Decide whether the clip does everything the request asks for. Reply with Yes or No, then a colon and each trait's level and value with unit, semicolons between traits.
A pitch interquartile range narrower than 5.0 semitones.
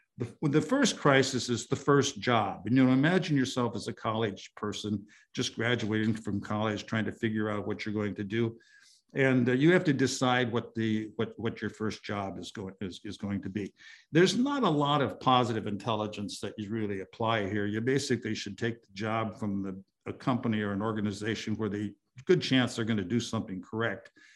Yes: average, 3.4 semitones